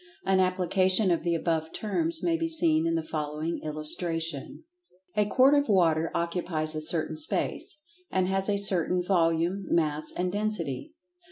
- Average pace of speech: Yes, average, 150 wpm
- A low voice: No, medium, 175 Hz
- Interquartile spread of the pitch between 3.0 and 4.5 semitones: Yes, average, 3.9 semitones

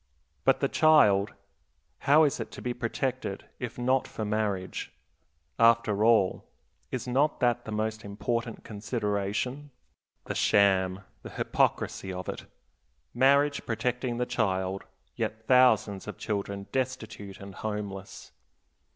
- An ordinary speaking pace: No, slow, 125 wpm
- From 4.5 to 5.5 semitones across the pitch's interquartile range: No, average, 3.8 semitones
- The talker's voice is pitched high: No, low, 110 Hz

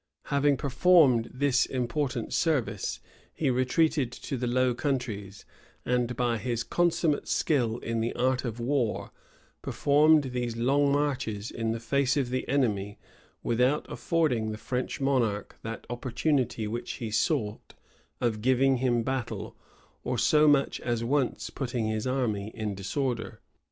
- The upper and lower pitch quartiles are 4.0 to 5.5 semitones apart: No, average, 3.3 semitones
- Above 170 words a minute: No, average, 140 wpm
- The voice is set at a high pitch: No, low, 125 Hz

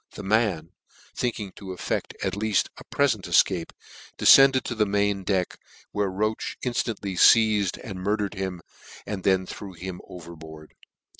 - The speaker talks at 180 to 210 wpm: No, average, 150 wpm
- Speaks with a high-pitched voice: No, low, 100 Hz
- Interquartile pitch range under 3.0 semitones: Yes, narrow, 2.6 semitones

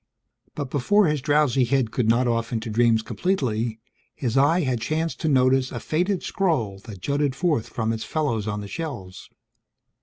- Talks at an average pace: Yes, average, 175 wpm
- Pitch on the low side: Yes, low, 130 Hz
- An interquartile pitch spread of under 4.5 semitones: No, average, 5.1 semitones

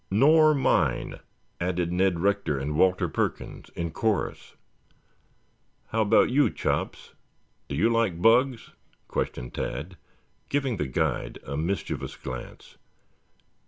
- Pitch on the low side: Yes, very low, 95 Hz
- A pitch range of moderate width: No, wide, 5.7 semitones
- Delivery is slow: Yes, slow, 115 wpm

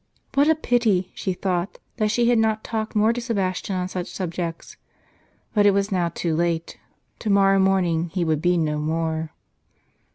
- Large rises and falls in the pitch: No, average, 4.0 semitones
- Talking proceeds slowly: No, average, 175 wpm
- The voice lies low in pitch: No, high, 190 Hz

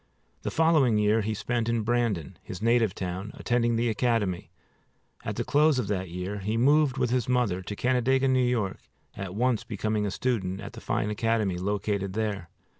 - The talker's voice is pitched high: No, low, 110 Hz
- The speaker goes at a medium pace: Yes, average, 185 wpm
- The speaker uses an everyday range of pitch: Yes, average, 3.7 semitones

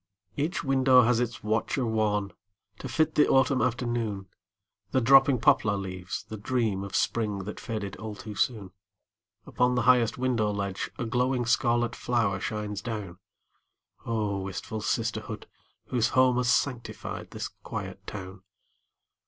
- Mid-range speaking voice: No, low, 115 Hz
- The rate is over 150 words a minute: No, average, 140 wpm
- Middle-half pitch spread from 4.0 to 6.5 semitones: No, average, 3.3 semitones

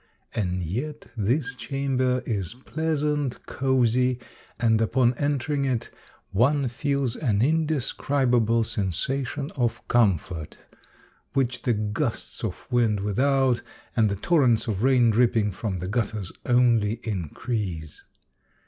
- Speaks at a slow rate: Yes, slow, 115 wpm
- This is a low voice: Yes, low, 120 Hz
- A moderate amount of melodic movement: Yes, average, 4.2 semitones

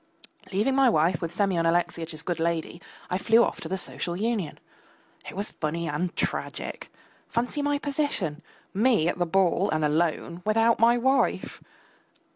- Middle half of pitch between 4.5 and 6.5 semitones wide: Yes, wide, 5.6 semitones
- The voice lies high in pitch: No, medium, 180 Hz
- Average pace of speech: Yes, average, 155 wpm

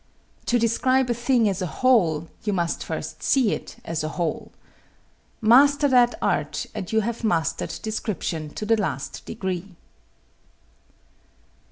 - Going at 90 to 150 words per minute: Yes, average, 140 wpm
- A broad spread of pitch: Yes, wide, 5.9 semitones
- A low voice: No, high, 215 Hz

